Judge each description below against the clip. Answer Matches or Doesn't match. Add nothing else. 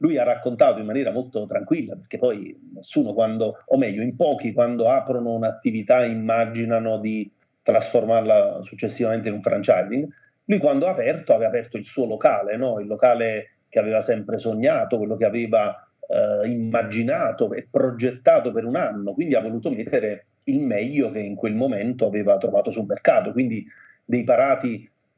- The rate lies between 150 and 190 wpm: Matches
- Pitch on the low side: Matches